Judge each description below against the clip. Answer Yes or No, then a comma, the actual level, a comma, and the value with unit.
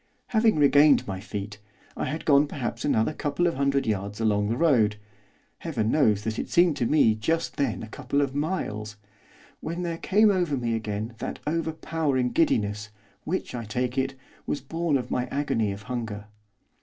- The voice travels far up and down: Yes, wide, 6.2 semitones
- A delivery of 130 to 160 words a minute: No, average, 175 wpm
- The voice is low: Yes, low, 130 Hz